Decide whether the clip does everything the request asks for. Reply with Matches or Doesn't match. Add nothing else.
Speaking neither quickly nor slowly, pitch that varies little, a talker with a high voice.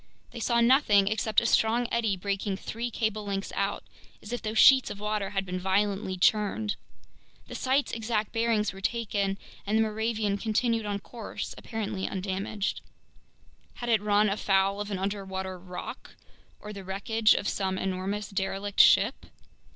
Matches